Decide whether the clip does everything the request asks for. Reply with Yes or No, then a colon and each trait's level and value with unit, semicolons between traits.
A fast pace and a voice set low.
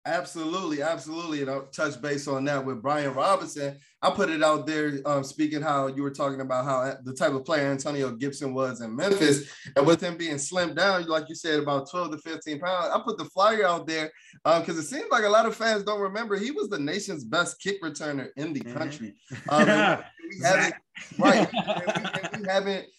No: fast, 220 wpm; medium, 155 Hz